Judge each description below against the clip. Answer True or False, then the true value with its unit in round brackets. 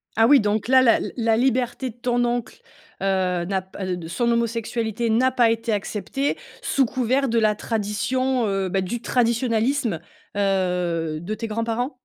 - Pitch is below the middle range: False (225 Hz)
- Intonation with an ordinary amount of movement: True (3.8 semitones)